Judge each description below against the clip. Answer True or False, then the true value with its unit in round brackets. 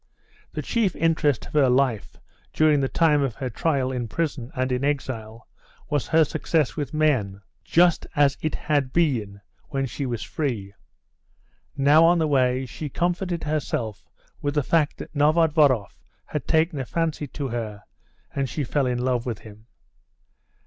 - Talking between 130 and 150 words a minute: False (165 wpm)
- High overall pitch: False (140 Hz)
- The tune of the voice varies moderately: True (3.9 semitones)